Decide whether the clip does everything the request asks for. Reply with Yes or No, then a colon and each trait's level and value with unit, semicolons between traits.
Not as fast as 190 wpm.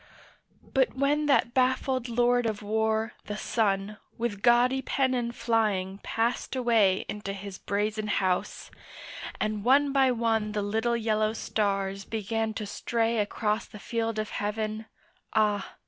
Yes: slow, 135 wpm